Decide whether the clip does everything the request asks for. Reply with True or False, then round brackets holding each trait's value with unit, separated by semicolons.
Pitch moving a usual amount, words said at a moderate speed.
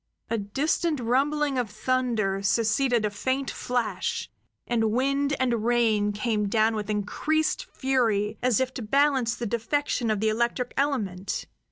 True (3.7 semitones; 145 wpm)